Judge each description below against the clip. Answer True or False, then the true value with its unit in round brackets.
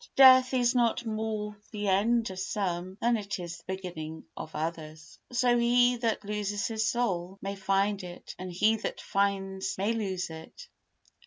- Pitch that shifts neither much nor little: True (3.7 semitones)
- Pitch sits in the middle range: False (200 Hz)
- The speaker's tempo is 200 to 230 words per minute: False (165 wpm)